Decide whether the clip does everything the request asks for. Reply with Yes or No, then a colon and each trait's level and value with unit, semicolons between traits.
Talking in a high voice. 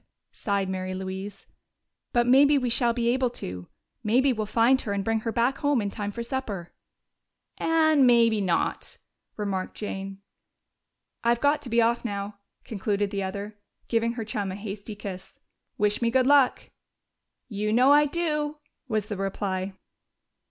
Yes: high, 220 Hz